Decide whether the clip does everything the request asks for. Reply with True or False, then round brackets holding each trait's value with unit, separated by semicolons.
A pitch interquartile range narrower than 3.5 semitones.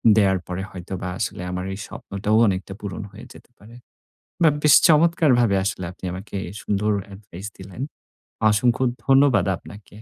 False (3.8 semitones)